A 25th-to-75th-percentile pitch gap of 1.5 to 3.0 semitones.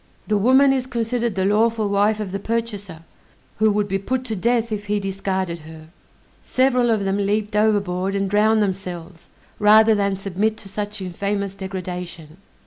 Yes: narrow, 2.4 semitones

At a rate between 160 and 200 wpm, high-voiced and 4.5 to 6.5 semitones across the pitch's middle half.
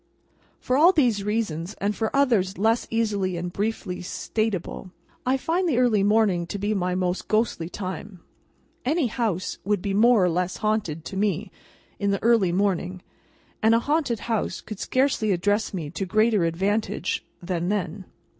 No: average, 165 wpm; high, 205 Hz; average, 3.5 semitones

